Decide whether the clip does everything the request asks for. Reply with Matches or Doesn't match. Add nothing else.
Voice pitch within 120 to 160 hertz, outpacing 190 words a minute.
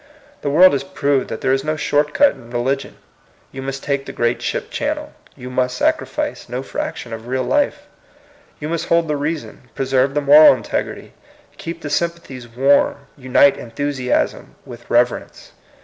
Doesn't match